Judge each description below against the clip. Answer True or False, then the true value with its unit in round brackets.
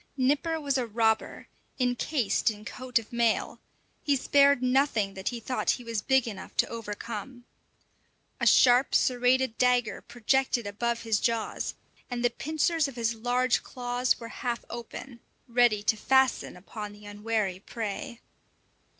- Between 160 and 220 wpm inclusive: False (145 wpm)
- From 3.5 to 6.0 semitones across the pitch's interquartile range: False (2.6 semitones)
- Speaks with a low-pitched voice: False (240 Hz)